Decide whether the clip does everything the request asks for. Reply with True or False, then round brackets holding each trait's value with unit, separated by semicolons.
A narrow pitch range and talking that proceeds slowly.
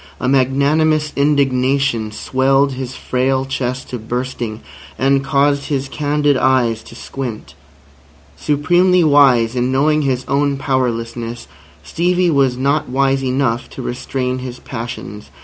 True (2.2 semitones; 125 wpm)